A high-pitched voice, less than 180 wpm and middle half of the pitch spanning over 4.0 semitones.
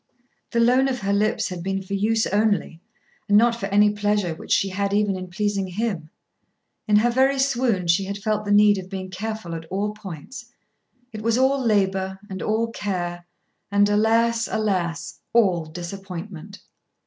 No: high, 205 Hz; average, 170 wpm; average, 2.7 semitones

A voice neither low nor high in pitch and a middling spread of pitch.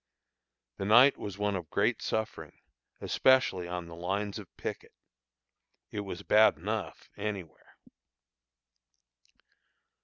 No: low, 100 Hz; average, 3.1 semitones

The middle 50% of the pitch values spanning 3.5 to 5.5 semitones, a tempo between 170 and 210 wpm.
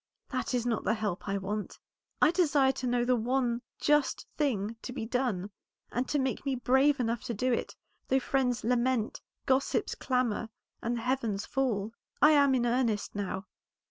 No: average, 3.0 semitones; average, 175 wpm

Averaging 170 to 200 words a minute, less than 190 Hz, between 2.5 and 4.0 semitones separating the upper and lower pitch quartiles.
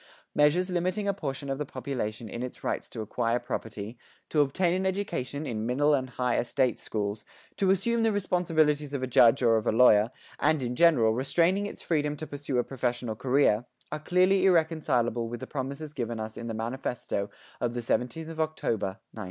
No: average, 195 wpm; low, 135 Hz; average, 5.3 semitones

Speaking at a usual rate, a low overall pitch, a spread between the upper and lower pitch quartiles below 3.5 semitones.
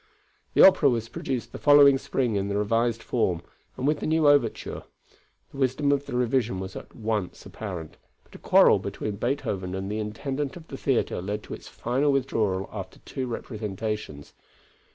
No: average, 175 wpm; low, 115 Hz; average, 4.9 semitones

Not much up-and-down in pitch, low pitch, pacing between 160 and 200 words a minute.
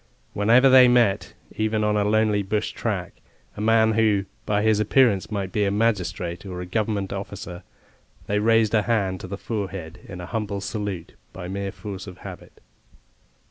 Yes: narrow, 2.2 semitones; low, 105 Hz; average, 175 wpm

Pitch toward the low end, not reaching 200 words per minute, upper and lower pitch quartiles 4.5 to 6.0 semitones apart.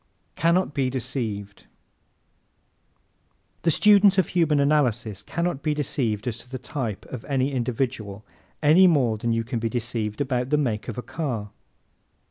Yes: low, 130 Hz; average, 160 wpm; average, 4.8 semitones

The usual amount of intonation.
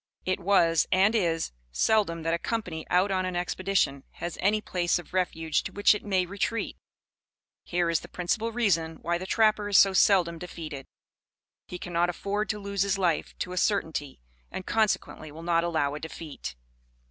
Yes: average, 3.2 semitones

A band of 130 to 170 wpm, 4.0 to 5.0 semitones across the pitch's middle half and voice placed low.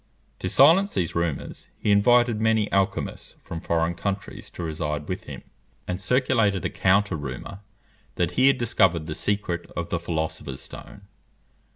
Yes: average, 155 wpm; average, 4.5 semitones; very low, 95 Hz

